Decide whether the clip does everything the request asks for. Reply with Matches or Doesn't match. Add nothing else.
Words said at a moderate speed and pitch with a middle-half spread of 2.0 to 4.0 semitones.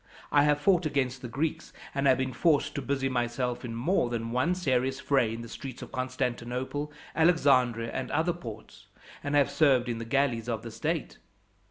Matches